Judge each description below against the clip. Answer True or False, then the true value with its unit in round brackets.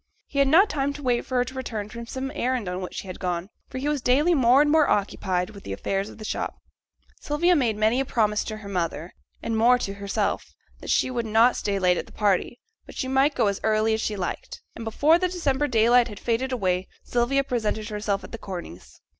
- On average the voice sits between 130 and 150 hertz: False (230 Hz)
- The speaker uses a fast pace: True (235 wpm)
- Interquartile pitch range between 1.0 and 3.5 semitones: False (4.7 semitones)